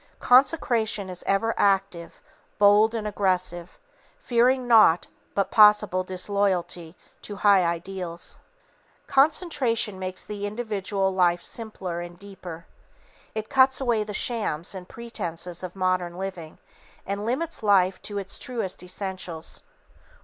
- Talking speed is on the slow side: Yes, slow, 120 wpm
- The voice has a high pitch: Yes, high, 195 Hz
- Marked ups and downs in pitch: No, average, 3.4 semitones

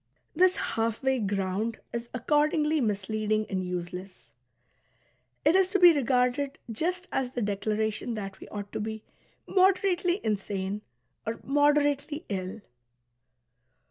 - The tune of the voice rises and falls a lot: Yes, wide, 6.3 semitones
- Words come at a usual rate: No, slow, 120 wpm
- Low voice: No, high, 230 Hz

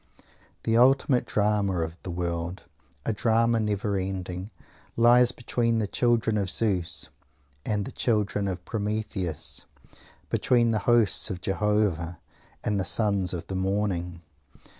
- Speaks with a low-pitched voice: Yes, low, 105 Hz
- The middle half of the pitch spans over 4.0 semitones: No, average, 3.7 semitones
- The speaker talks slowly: Yes, slow, 130 wpm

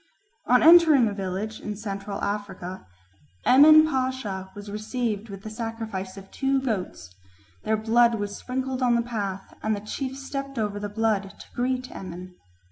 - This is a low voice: No, high, 220 Hz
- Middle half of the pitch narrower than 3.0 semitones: No, average, 4.2 semitones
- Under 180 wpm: Yes, average, 160 wpm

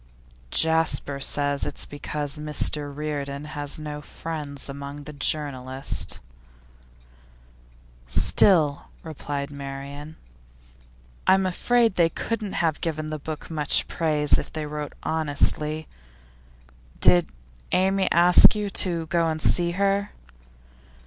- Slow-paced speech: Yes, slow, 110 wpm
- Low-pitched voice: No, medium, 150 Hz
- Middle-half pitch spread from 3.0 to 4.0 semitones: No, narrow, 2.6 semitones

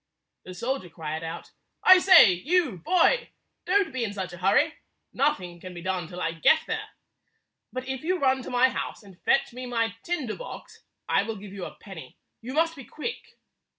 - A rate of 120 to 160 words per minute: No, average, 195 wpm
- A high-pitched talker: Yes, high, 235 Hz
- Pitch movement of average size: No, wide, 8.6 semitones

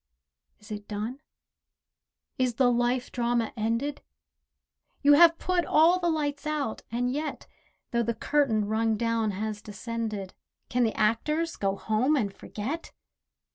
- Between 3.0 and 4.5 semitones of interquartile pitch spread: No, average, 5.0 semitones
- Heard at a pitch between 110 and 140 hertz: No, high, 235 Hz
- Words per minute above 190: No, slow, 135 wpm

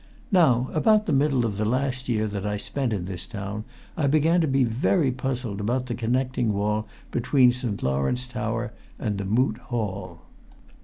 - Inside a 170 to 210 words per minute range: Yes, average, 175 wpm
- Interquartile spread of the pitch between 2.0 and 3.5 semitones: No, average, 4.0 semitones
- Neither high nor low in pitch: No, low, 120 Hz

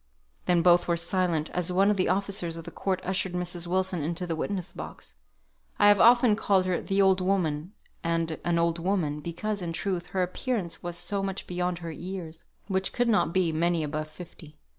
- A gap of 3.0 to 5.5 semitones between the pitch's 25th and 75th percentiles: No, narrow, 2.4 semitones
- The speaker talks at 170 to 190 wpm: No, average, 200 wpm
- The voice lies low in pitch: No, medium, 180 Hz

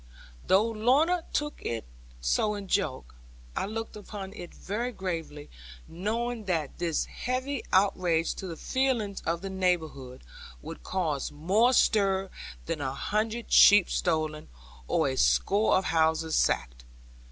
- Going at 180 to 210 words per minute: No, slow, 135 wpm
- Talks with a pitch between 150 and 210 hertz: Yes, high, 190 Hz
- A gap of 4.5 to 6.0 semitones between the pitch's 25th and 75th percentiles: Yes, average, 5.3 semitones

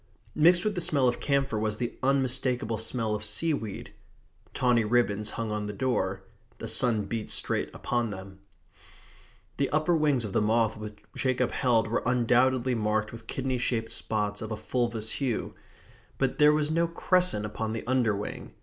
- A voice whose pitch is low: Yes, low, 120 Hz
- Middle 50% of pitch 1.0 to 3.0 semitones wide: No, average, 3.5 semitones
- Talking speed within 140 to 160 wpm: No, average, 170 wpm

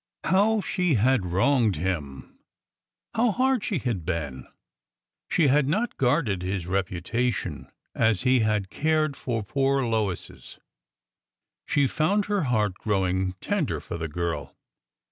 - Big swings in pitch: Yes, wide, 8.6 semitones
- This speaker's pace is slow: Yes, slow, 130 wpm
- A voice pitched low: Yes, low, 120 Hz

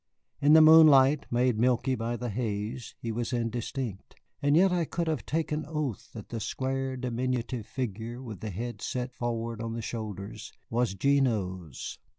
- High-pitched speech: No, low, 120 Hz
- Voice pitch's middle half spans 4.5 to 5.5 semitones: No, average, 3.1 semitones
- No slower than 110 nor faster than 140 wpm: No, average, 160 wpm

